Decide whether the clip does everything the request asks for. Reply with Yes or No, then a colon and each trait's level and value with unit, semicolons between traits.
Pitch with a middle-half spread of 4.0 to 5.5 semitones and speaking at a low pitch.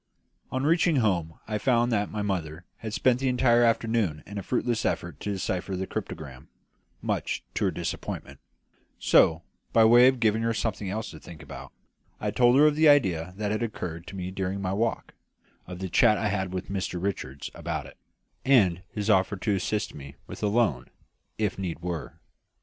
Yes: average, 4.4 semitones; low, 100 Hz